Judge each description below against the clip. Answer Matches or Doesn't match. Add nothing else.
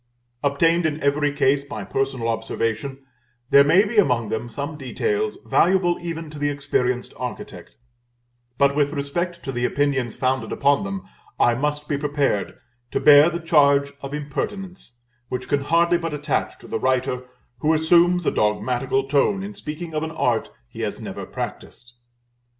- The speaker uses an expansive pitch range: Doesn't match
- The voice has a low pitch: Doesn't match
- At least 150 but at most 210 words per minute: Matches